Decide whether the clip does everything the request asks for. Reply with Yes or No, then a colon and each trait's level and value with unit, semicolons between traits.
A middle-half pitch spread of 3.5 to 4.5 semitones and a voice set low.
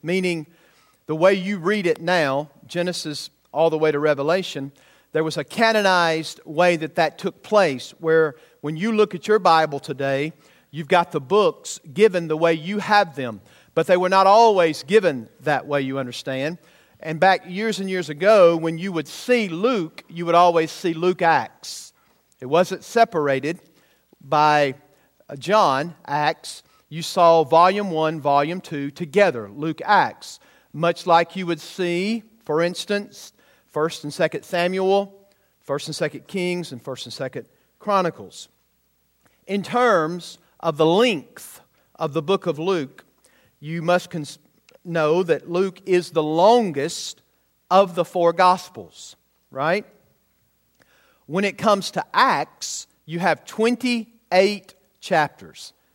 No: average, 3.8 semitones; medium, 170 Hz